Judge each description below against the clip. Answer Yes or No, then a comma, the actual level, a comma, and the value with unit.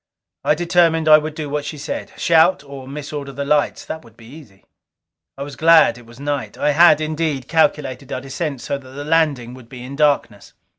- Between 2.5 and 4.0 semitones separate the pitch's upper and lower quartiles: Yes, average, 2.8 semitones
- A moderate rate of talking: No, fast, 210 wpm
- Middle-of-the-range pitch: Yes, medium, 145 Hz